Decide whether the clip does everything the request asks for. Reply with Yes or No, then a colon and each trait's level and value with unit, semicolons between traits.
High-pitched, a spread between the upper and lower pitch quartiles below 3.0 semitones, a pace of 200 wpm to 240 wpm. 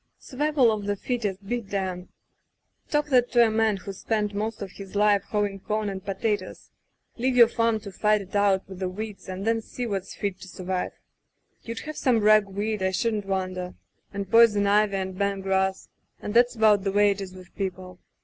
Yes: high, 205 Hz; narrow, 2.5 semitones; fast, 205 wpm